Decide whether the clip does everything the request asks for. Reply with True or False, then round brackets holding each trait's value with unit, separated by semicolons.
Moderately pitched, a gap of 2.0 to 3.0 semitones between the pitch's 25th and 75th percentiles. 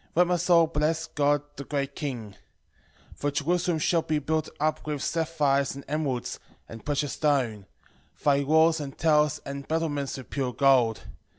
True (145 Hz; 2.5 semitones)